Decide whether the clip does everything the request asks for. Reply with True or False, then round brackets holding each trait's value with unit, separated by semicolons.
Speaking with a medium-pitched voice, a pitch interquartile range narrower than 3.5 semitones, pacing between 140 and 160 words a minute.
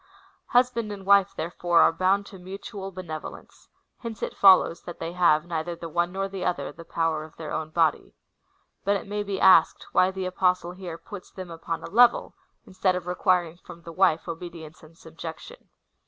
False (180 Hz; 2.6 semitones; 185 wpm)